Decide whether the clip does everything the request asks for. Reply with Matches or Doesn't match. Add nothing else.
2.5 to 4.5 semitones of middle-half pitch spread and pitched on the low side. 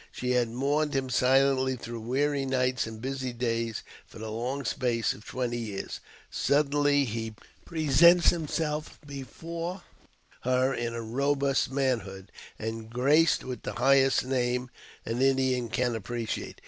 Matches